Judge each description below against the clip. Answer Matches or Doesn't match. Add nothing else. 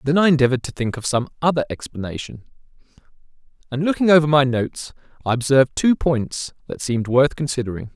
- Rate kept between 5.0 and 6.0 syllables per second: Doesn't match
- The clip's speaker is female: Doesn't match